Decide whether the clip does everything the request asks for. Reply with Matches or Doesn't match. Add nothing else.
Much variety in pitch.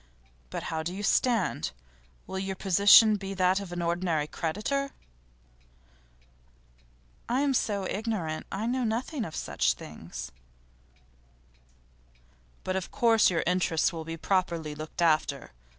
Doesn't match